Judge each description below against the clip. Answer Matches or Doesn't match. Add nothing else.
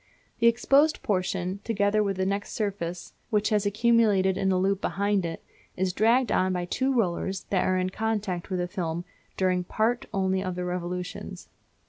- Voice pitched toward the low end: Doesn't match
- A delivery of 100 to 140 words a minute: Doesn't match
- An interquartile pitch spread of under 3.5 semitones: Matches